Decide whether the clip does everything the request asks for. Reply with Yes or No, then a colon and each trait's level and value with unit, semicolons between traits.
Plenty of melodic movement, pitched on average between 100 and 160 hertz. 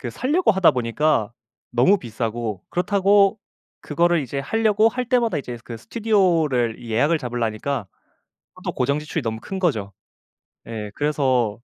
Yes: wide, 8.5 semitones; medium, 140 Hz